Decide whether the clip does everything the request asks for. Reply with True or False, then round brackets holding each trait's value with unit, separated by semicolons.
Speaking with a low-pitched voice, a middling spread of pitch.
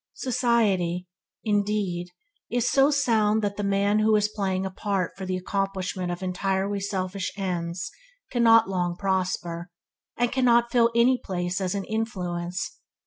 False (195 Hz; 3.2 semitones)